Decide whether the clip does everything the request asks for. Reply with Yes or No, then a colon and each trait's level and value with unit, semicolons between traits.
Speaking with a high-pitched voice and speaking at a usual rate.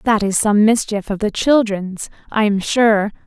Yes: high, 210 Hz; average, 185 wpm